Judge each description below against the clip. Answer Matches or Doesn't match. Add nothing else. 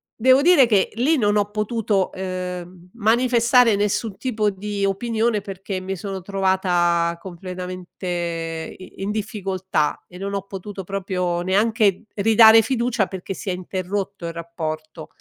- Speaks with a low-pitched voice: Doesn't match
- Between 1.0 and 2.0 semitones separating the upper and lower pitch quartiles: Doesn't match